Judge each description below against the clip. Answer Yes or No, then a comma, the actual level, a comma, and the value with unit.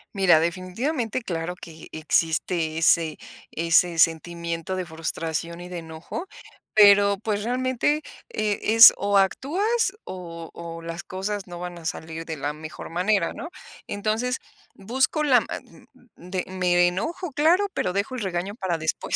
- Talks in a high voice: No, medium, 180 Hz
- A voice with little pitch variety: No, average, 4.6 semitones